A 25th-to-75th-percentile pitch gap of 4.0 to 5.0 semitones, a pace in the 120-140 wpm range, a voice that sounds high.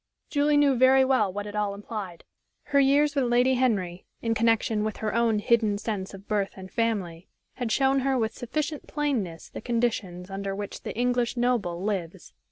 No: average, 4.5 semitones; average, 180 wpm; high, 225 Hz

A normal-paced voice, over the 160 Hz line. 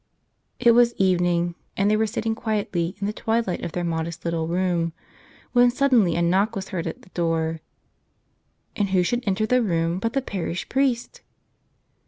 Yes: average, 180 wpm; high, 190 Hz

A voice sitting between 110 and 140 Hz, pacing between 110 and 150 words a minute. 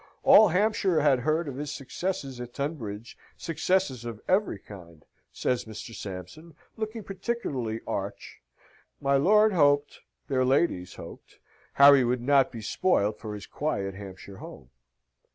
Yes: low, 135 Hz; slow, 135 wpm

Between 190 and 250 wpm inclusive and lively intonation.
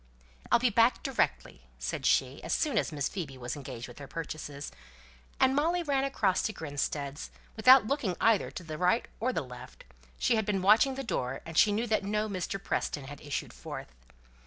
Yes: average, 195 wpm; wide, 8.4 semitones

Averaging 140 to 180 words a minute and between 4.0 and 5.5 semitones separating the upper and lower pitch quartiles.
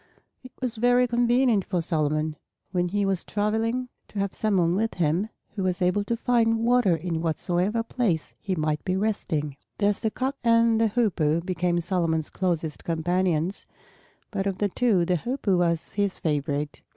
Yes: average, 170 wpm; average, 5.1 semitones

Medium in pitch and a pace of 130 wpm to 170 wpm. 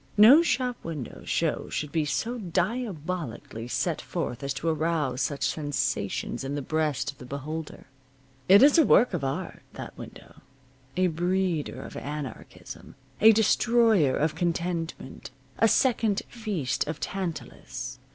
Yes: medium, 165 Hz; average, 140 wpm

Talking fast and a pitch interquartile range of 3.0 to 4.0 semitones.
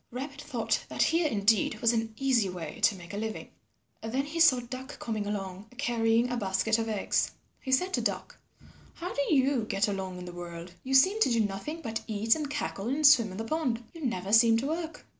No: fast, 215 wpm; average, 5.2 semitones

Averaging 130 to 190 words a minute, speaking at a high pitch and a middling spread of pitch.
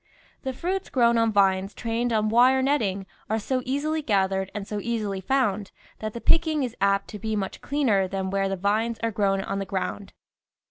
No: average, 200 wpm; high, 215 Hz; average, 4.2 semitones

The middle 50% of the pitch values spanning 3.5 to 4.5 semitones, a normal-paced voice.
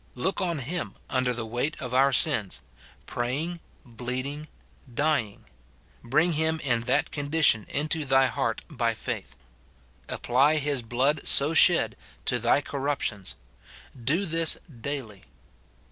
No: average, 4.1 semitones; slow, 130 wpm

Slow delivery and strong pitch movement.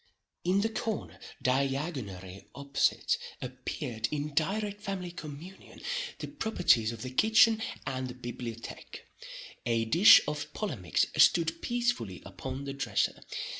Yes: slow, 120 wpm; wide, 8.2 semitones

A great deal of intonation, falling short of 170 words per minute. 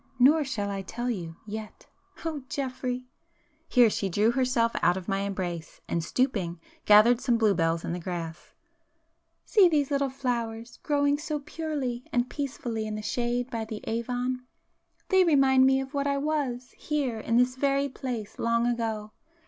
No: average, 4.4 semitones; average, 155 wpm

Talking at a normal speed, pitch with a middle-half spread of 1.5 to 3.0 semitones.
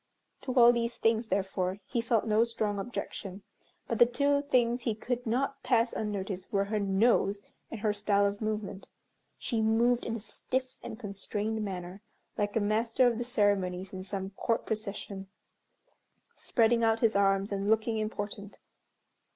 Yes: average, 160 wpm; average, 2.7 semitones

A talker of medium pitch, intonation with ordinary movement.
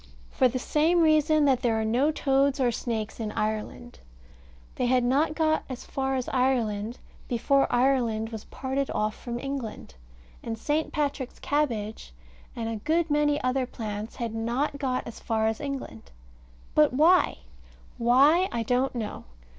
No: very high, 255 Hz; average, 4.0 semitones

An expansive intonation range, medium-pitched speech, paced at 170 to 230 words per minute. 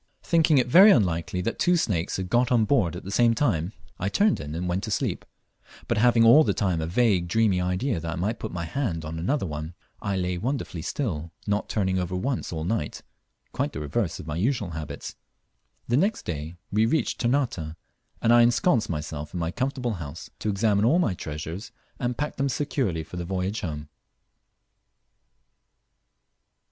No: wide, 6.4 semitones; very low, 95 Hz; average, 190 wpm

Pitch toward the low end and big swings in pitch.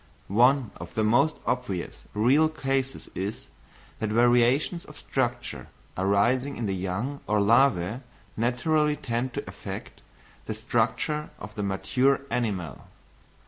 No: low, 120 Hz; average, 4.6 semitones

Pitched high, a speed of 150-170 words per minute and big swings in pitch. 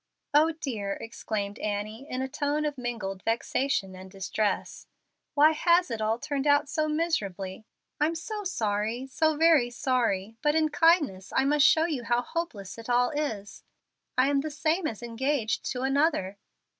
Yes: very high, 260 Hz; average, 165 wpm; wide, 6.0 semitones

